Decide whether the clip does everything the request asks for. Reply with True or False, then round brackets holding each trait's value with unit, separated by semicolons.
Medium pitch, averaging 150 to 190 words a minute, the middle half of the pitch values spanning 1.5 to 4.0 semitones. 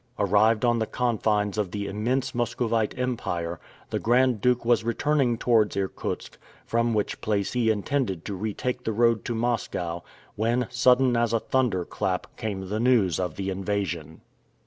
False (110 Hz; 160 wpm; 3.3 semitones)